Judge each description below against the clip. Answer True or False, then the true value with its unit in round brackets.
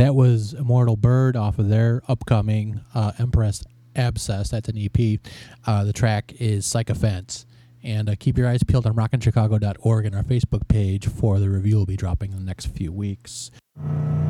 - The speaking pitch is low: True (110 Hz)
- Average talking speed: True (180 wpm)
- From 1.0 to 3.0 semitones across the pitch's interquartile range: True (2.7 semitones)